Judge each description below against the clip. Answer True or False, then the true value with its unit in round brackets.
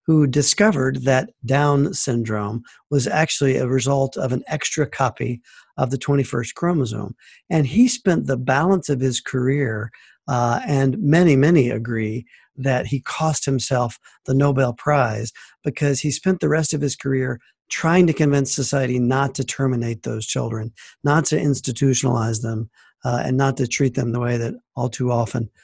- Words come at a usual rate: True (165 wpm)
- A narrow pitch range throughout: False (3.1 semitones)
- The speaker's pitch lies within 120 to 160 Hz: True (135 Hz)